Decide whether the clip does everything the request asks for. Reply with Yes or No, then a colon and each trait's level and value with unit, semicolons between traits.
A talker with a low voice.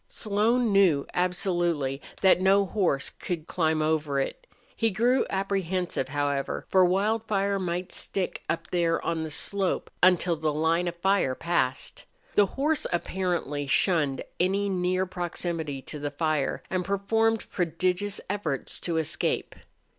No: medium, 180 Hz